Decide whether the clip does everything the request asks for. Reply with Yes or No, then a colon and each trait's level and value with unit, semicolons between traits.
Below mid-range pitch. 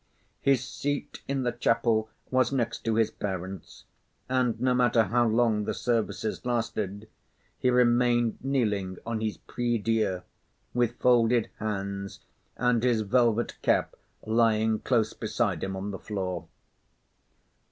Yes: low, 115 Hz